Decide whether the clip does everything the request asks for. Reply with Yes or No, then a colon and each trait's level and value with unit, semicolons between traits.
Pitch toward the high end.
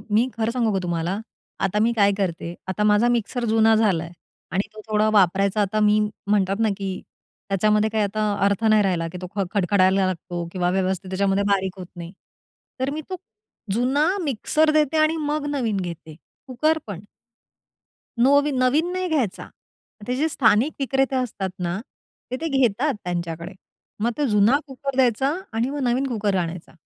Yes: high, 210 Hz